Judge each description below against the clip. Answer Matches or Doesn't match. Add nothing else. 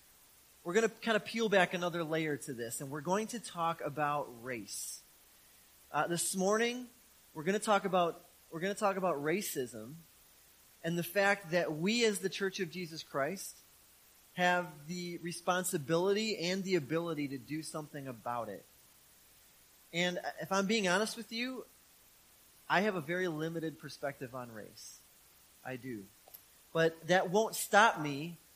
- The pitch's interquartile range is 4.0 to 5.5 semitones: Matches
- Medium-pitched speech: Matches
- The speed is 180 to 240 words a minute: Doesn't match